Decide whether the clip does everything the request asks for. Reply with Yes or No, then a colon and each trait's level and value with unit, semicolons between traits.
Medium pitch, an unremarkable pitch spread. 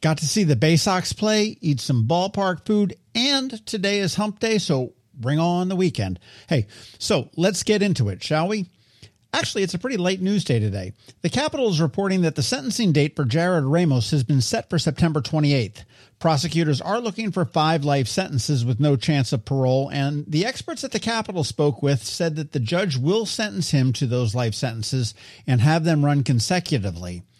No: medium, 155 Hz; wide, 6.3 semitones